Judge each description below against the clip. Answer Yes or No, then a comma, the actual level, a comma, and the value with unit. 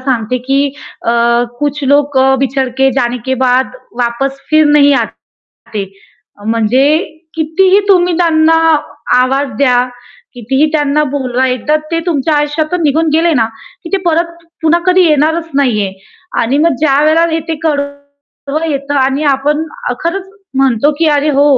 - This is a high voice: Yes, very high, 285 Hz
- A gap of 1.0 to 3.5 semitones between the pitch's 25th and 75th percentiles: Yes, average, 3.2 semitones